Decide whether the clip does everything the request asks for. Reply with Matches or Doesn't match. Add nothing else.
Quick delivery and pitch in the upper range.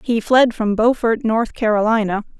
Doesn't match